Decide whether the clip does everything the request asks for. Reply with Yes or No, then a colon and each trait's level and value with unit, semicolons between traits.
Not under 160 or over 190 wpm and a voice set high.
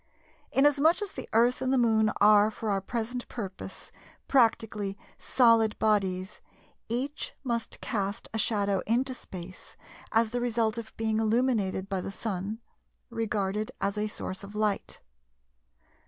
No: average, 140 wpm; high, 220 Hz